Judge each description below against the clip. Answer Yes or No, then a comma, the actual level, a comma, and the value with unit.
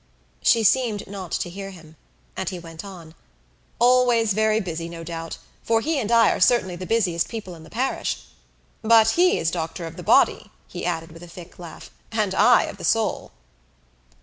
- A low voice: No, high, 190 Hz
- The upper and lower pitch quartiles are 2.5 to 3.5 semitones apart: No, average, 5.2 semitones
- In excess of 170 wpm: Yes, average, 190 wpm